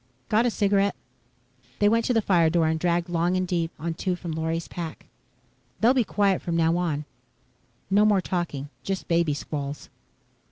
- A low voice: No, medium, 175 Hz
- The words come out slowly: No, average, 175 wpm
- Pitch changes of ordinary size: Yes, average, 3.4 semitones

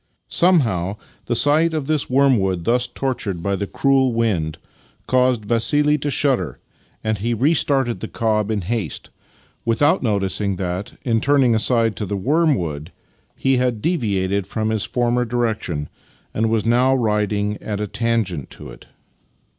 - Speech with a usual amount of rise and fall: Yes, average, 4.3 semitones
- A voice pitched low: Yes, low, 115 Hz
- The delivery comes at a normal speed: Yes, average, 160 wpm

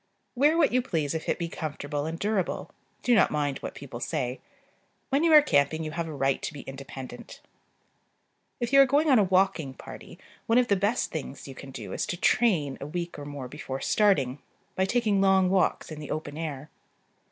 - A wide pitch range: Yes, wide, 6.7 semitones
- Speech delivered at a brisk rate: Yes, fast, 210 wpm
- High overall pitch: No, medium, 165 Hz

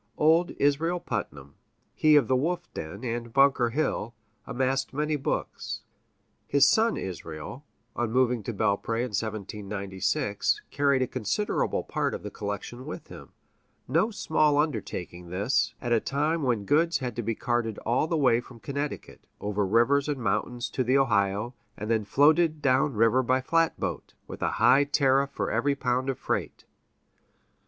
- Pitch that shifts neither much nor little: Yes, average, 4.6 semitones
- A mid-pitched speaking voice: No, low, 130 Hz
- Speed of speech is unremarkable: Yes, average, 160 wpm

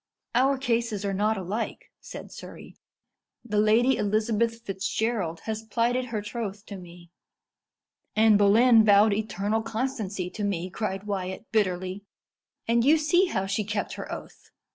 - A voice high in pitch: Yes, high, 215 Hz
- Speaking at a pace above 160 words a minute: No, average, 140 wpm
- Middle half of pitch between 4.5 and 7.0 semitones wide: No, average, 2.8 semitones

